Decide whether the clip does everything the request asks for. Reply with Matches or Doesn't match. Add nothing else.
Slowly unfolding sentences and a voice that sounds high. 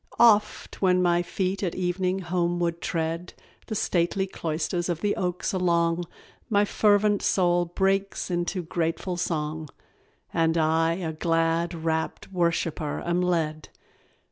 Doesn't match